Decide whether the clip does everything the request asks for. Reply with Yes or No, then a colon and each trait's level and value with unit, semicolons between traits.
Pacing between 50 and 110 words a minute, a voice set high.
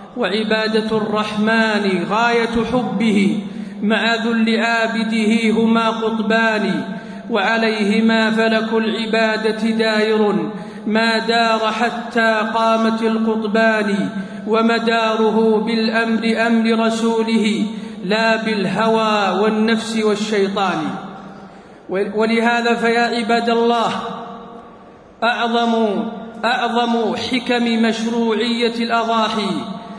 Yes: average, 70 wpm; high, 225 Hz